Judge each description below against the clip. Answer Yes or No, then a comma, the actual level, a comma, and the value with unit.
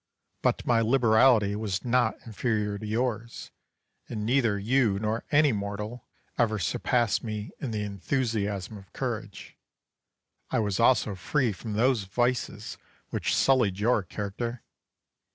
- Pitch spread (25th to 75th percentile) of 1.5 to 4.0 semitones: Yes, average, 3.0 semitones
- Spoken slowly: Yes, slow, 130 wpm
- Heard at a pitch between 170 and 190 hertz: No, low, 110 Hz